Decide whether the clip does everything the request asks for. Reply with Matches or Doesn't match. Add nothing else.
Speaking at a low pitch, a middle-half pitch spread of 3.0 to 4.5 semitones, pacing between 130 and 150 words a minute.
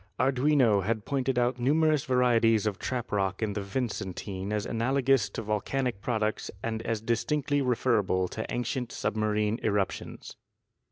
Matches